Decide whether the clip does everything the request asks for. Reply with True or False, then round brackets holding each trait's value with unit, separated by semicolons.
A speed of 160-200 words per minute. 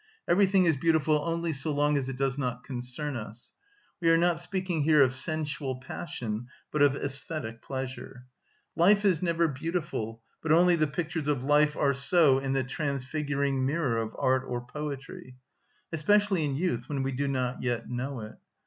True (175 wpm)